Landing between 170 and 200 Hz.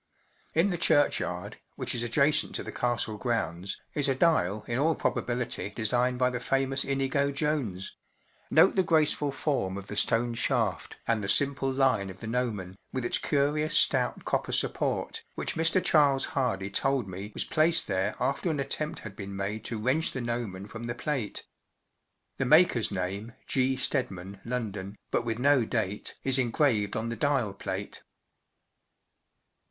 No: low, 125 Hz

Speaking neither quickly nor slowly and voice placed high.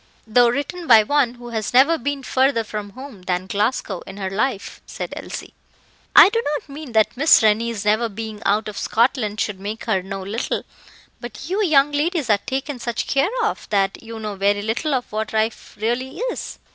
Yes: average, 195 wpm; high, 230 Hz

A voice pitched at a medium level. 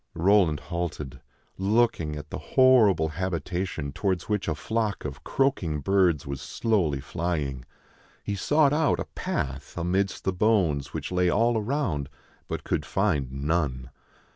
No: very low, 90 Hz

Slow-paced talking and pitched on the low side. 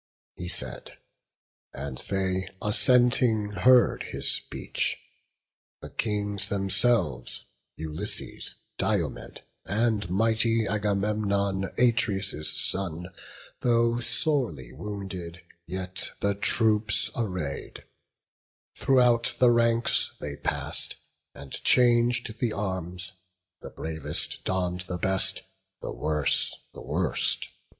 Yes: slow, 95 wpm; low, 100 Hz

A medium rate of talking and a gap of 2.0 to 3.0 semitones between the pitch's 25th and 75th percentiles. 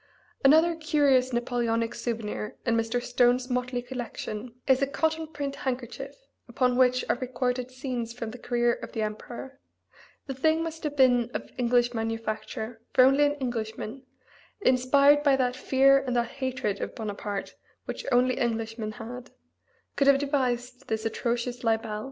Yes: average, 150 wpm; narrow, 2.5 semitones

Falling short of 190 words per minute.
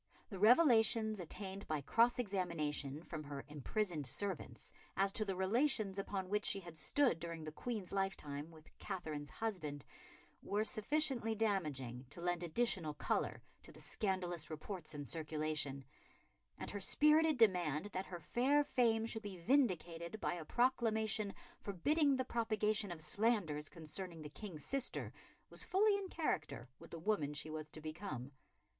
Yes: average, 150 wpm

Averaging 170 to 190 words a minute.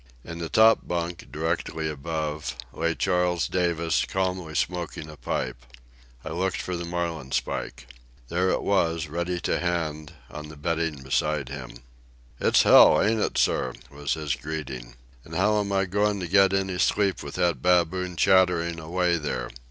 No: average, 160 wpm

